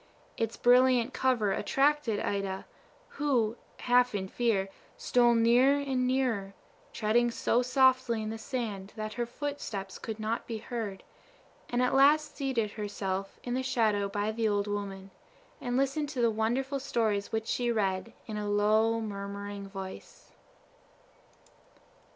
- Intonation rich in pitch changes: No, average, 3.5 semitones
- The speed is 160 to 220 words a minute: No, average, 145 wpm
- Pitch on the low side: No, high, 225 Hz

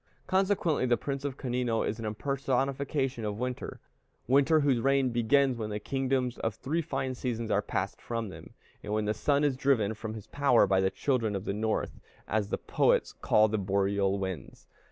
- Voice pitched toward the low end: Yes, low, 120 Hz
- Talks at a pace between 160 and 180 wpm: No, average, 195 wpm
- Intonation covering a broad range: No, average, 4.3 semitones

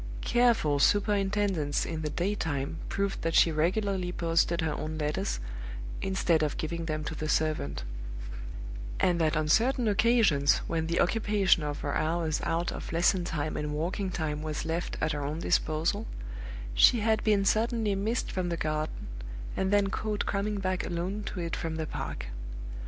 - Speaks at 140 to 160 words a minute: No, average, 170 wpm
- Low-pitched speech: No, medium, 170 Hz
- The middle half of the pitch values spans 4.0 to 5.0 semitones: Yes, average, 4.4 semitones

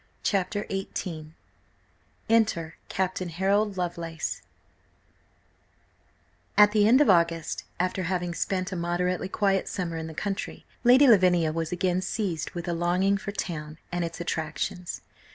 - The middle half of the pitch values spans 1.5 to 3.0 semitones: Yes, narrow, 2.6 semitones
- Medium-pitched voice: Yes, medium, 180 Hz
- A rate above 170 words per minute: No, slow, 135 wpm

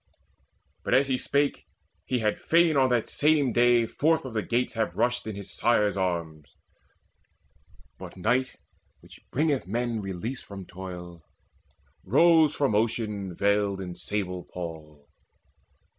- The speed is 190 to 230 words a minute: No, average, 140 wpm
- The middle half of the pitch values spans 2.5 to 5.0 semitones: No, wide, 5.4 semitones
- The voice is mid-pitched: No, low, 110 Hz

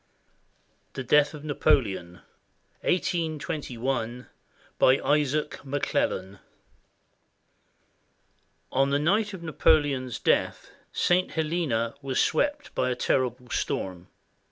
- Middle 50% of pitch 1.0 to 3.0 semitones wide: No, average, 4.1 semitones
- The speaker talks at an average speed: No, slow, 85 wpm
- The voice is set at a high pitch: No, medium, 140 Hz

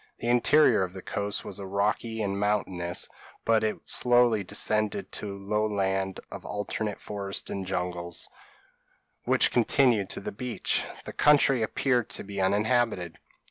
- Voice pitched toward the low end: Yes, low, 105 Hz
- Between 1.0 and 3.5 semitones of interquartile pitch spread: Yes, average, 2.9 semitones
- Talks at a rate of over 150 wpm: No, average, 140 wpm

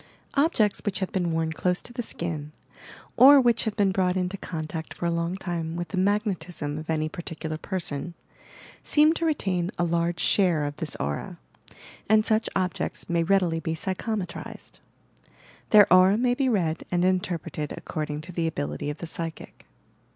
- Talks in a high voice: No, medium, 175 Hz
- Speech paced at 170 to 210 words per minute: Yes, average, 175 wpm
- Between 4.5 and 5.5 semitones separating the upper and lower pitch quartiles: No, average, 3.6 semitones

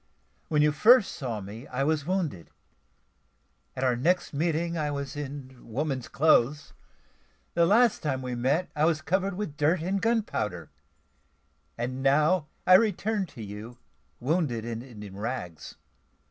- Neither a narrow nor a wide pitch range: No, wide, 5.7 semitones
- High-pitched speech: No, medium, 145 Hz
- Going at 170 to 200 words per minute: No, average, 145 wpm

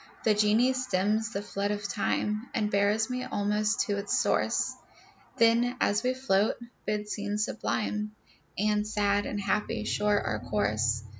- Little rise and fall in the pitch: Yes, narrow, 1.4 semitones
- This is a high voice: Yes, high, 210 Hz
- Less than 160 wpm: Yes, average, 150 wpm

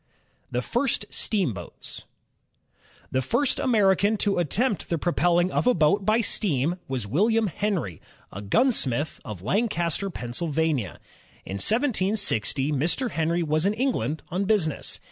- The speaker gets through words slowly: Yes, slow, 130 wpm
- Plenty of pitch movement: Yes, wide, 6.8 semitones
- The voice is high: No, medium, 175 Hz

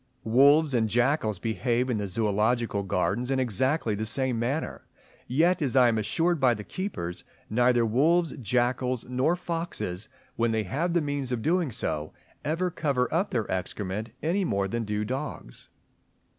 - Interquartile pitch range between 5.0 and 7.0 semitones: Yes, wide, 5.6 semitones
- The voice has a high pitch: No, low, 125 Hz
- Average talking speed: Yes, average, 160 wpm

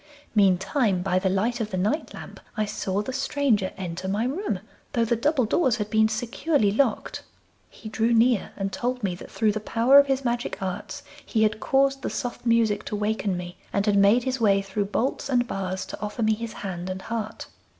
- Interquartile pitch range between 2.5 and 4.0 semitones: Yes, average, 3.6 semitones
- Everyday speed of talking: No, fast, 210 wpm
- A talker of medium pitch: No, high, 215 Hz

